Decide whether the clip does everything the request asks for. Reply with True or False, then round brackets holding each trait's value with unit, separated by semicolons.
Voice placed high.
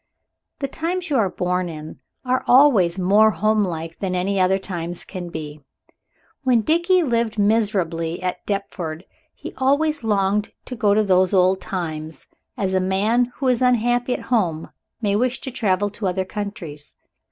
True (200 Hz)